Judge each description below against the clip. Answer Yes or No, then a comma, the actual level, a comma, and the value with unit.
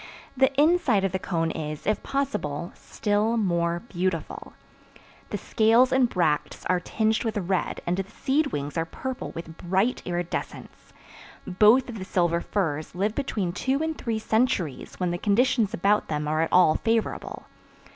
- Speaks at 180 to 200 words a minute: No, average, 160 wpm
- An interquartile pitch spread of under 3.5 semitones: No, average, 5.2 semitones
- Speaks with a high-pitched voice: Yes, high, 195 Hz